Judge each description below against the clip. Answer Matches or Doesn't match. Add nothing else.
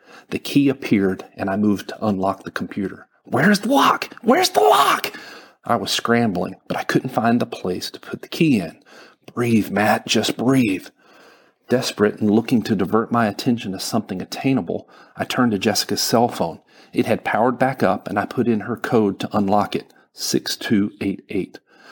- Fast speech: Doesn't match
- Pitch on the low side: Matches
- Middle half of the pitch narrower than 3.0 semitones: Doesn't match